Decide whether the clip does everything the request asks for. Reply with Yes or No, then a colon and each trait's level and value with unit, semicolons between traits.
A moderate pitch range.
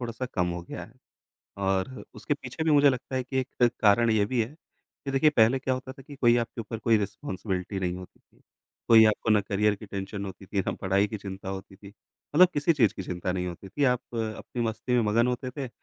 Yes: average, 4.7 semitones